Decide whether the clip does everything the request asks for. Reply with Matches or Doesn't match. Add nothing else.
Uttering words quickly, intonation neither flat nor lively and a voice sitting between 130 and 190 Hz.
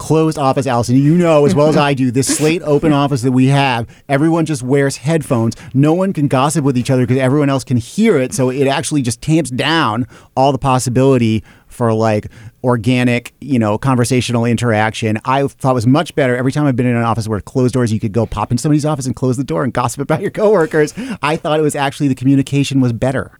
Matches